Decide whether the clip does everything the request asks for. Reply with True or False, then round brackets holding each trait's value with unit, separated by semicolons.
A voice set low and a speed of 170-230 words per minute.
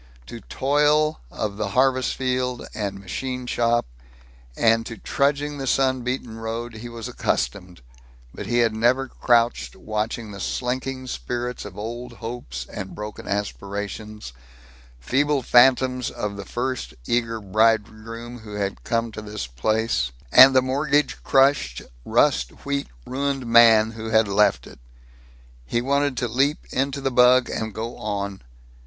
False (115 Hz; 145 wpm)